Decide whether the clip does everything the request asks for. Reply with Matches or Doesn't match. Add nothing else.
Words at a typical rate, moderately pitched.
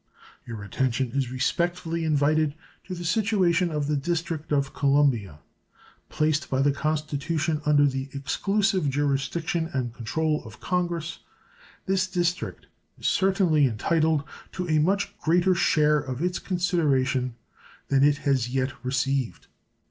Doesn't match